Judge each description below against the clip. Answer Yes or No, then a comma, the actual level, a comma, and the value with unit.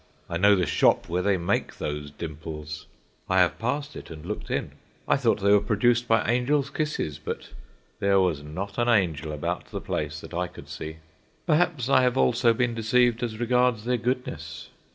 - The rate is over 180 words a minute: Yes, average, 190 wpm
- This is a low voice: Yes, low, 105 Hz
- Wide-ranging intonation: Yes, wide, 6.7 semitones